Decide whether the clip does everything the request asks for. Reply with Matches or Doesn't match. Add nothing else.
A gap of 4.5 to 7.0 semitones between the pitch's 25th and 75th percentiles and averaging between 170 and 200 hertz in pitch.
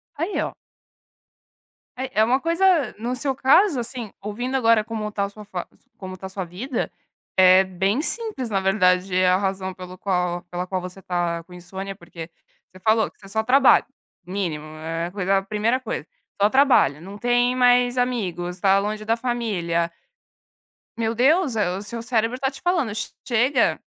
Doesn't match